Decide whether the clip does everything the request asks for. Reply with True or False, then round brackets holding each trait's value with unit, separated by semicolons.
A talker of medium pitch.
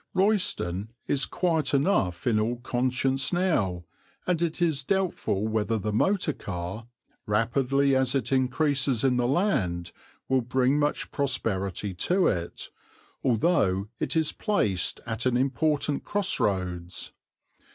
False (130 Hz)